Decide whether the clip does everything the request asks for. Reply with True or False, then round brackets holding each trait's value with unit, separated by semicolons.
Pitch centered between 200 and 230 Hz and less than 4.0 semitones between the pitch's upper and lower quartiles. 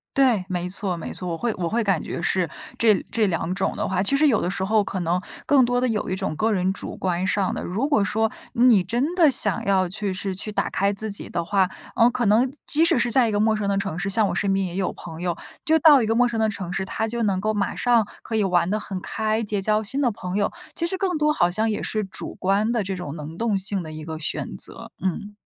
True (205 Hz; 3.5 semitones)